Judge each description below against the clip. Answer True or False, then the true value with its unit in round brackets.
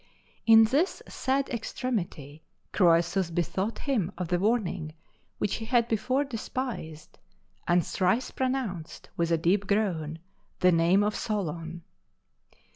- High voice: True (195 Hz)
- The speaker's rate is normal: False (120 wpm)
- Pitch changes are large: True (5.7 semitones)